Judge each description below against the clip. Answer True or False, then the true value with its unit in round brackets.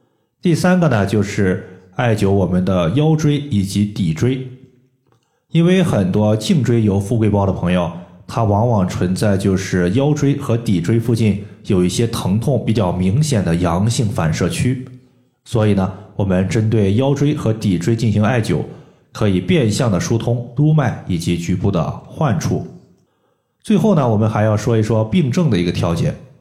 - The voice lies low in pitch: True (110 Hz)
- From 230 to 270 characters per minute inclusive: True (245 characters per minute)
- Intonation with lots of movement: False (4.8 semitones)